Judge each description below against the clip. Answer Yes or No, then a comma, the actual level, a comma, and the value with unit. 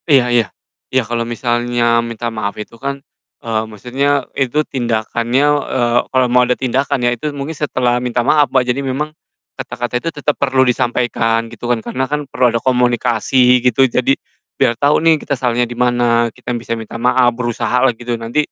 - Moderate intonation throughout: No, narrow, 2.1 semitones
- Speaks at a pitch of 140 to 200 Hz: No, low, 125 Hz